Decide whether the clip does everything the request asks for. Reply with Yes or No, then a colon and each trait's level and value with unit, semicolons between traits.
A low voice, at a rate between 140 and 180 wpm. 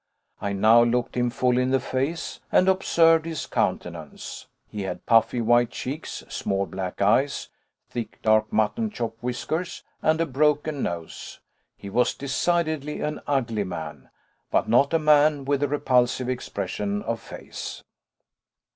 Yes: low, 125 Hz; average, 145 wpm